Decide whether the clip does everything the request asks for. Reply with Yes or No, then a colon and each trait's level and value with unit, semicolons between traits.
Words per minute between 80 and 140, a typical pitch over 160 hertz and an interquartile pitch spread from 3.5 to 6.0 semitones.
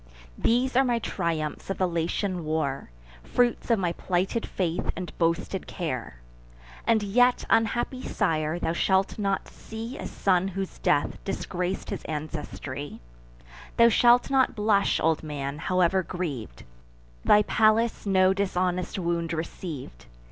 Yes: slow, 135 wpm; medium, 185 Hz; average, 4.6 semitones